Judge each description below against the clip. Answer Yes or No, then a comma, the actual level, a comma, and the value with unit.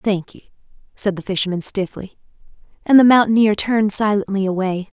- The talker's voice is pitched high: Yes, high, 205 Hz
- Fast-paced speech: No, average, 145 wpm